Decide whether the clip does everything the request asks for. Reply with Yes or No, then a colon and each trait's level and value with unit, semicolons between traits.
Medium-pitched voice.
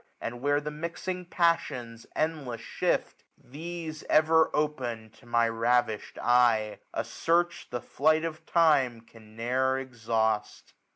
No: low, 130 Hz